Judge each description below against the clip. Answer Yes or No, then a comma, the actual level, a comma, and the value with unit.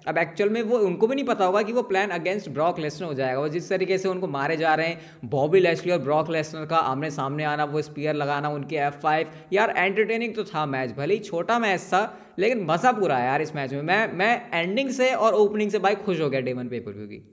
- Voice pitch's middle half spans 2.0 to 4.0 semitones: No, average, 5.2 semitones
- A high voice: No, medium, 165 Hz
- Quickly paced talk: Yes, fast, 255 wpm